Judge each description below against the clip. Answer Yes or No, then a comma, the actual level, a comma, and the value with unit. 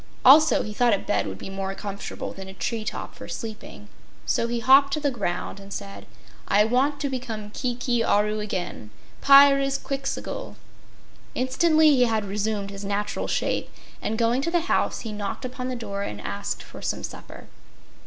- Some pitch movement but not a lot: Yes, average, 4.9 semitones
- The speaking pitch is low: No, high, 225 Hz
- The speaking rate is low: No, average, 175 wpm